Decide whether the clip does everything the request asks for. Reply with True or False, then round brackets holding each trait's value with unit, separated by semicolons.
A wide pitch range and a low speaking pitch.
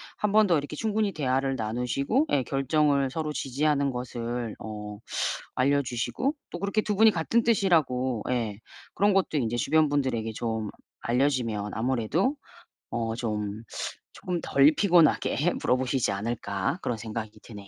True (5.9 semitones; 130 Hz)